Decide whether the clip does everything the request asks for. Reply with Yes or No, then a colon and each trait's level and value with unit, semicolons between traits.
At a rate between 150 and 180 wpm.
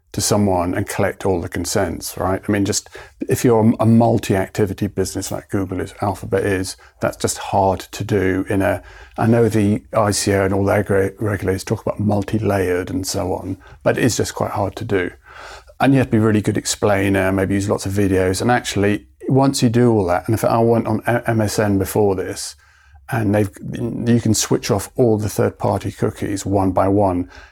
No: fast, 205 wpm